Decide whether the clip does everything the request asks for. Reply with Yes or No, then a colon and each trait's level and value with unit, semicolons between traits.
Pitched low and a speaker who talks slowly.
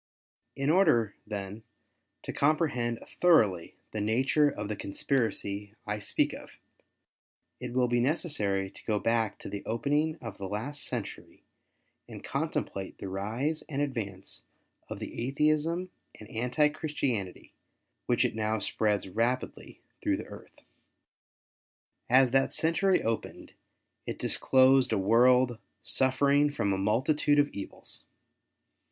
Yes: low, 120 Hz; slow, 130 wpm